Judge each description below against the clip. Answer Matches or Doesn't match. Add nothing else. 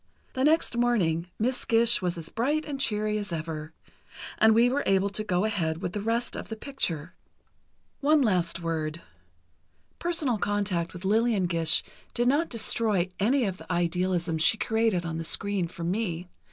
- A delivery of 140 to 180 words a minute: Matches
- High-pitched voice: Matches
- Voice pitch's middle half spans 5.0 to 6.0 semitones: Matches